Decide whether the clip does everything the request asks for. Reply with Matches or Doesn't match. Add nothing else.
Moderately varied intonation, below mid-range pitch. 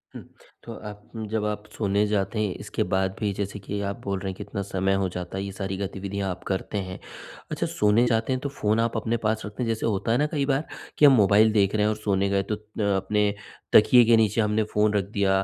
Doesn't match